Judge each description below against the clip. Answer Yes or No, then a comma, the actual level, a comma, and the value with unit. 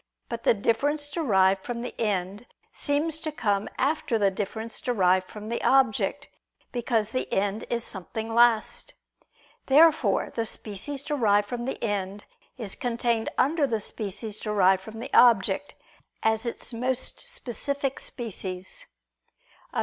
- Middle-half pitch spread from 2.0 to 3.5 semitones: No, average, 4.2 semitones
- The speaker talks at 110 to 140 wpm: Yes, slow, 135 wpm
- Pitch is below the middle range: No, high, 230 Hz